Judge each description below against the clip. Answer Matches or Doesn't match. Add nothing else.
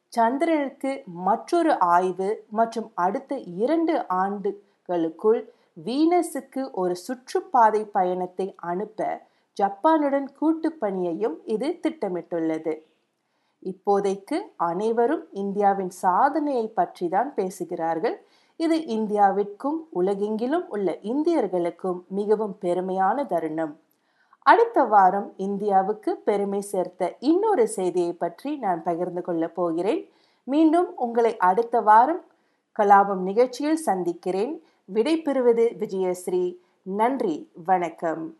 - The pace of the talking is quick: Doesn't match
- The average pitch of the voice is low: Doesn't match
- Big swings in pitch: Matches